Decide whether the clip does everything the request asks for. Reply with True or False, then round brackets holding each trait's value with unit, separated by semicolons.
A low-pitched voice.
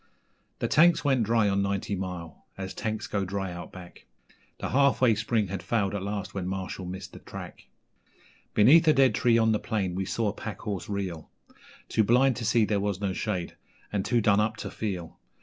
True (105 Hz)